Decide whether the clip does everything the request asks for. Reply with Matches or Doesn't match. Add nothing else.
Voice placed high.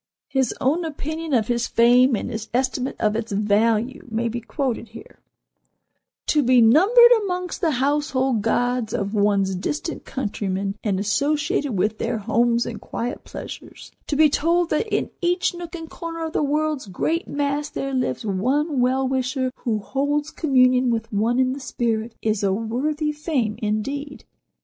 Matches